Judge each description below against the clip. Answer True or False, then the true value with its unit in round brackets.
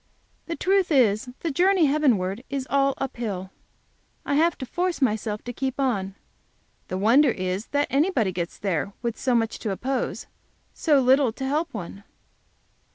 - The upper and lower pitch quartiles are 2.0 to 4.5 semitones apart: False (5.6 semitones)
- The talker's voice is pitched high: True (255 Hz)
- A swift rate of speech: False (160 wpm)